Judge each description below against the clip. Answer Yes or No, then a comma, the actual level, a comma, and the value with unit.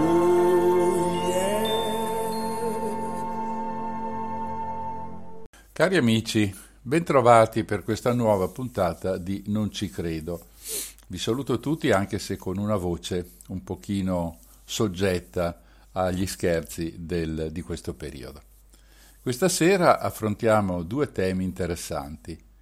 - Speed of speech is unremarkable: No, slow, 90 wpm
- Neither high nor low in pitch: No, low, 105 Hz